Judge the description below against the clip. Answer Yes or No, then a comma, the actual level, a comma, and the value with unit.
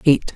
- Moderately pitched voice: Yes, medium, 145 Hz